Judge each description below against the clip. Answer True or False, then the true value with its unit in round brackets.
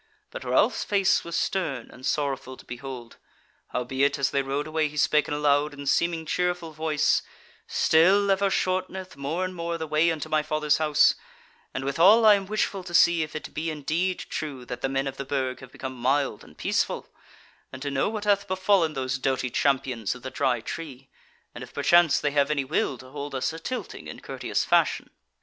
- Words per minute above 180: True (205 wpm)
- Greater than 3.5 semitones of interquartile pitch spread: True (4.2 semitones)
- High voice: False (150 Hz)